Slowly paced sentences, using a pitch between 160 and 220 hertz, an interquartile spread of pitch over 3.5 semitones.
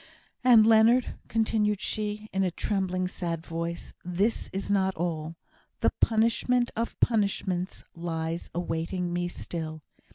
Yes: slow, 125 wpm; high, 190 Hz; average, 4.2 semitones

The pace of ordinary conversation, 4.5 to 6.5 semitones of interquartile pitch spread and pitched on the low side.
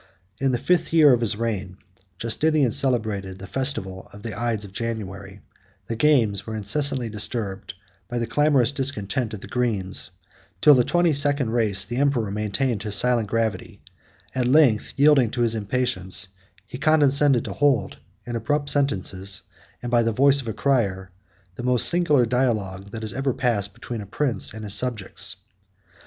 Yes: average, 170 wpm; average, 4.9 semitones; low, 115 Hz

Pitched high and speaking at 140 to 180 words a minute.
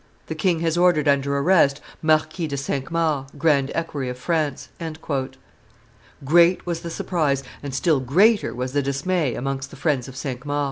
No: medium, 145 Hz; average, 170 wpm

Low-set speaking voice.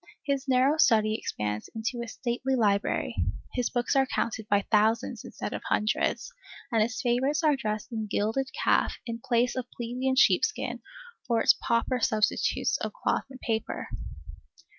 No: high, 235 Hz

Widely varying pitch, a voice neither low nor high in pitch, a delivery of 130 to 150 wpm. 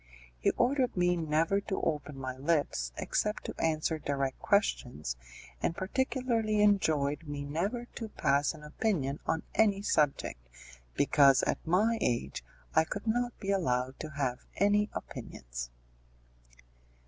Yes: wide, 6.8 semitones; medium, 160 Hz; slow, 135 wpm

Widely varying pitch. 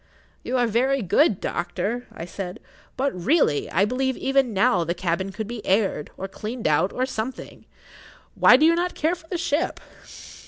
Yes: wide, 6.1 semitones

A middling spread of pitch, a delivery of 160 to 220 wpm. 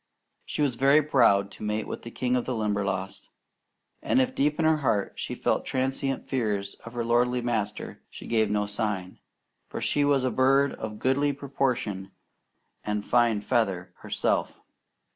Yes: average, 4.4 semitones; average, 165 wpm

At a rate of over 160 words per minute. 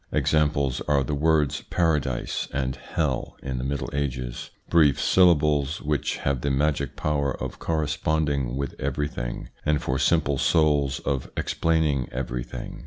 No: average, 140 wpm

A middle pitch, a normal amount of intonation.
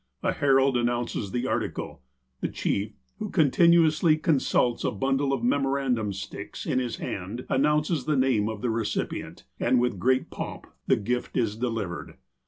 No: low, 125 Hz; average, 3.8 semitones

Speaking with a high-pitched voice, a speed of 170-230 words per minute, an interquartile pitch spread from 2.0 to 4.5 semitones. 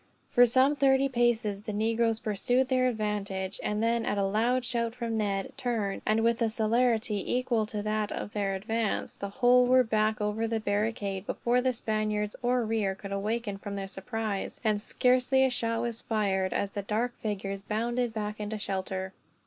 Yes: high, 220 Hz; average, 180 wpm; narrow, 2.6 semitones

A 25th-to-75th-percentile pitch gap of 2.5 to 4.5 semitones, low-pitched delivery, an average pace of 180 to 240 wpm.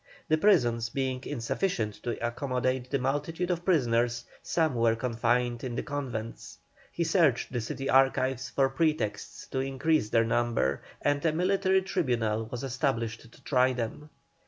No: average, 4.2 semitones; low, 130 Hz; average, 150 wpm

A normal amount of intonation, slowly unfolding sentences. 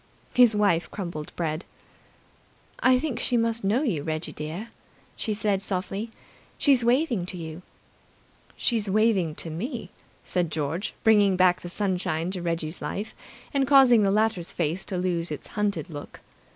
No: average, 4.8 semitones; average, 150 wpm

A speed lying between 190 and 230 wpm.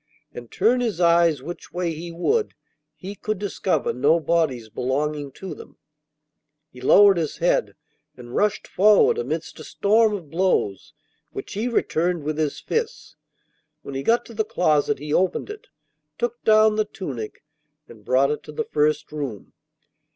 No: average, 160 wpm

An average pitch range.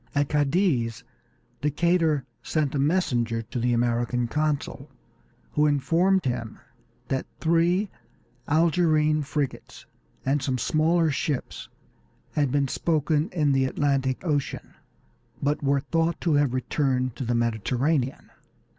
Yes: average, 3.6 semitones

